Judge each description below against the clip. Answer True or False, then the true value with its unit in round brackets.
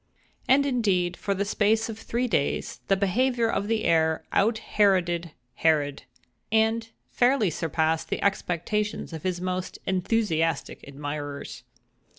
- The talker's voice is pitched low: False (190 Hz)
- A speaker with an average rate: False (130 wpm)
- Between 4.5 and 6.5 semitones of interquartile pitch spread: True (5.3 semitones)